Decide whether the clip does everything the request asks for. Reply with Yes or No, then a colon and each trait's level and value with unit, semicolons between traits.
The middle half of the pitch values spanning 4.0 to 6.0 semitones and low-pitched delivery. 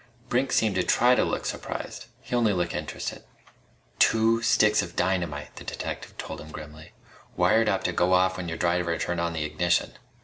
Yes: average, 4.3 semitones; very low, 90 Hz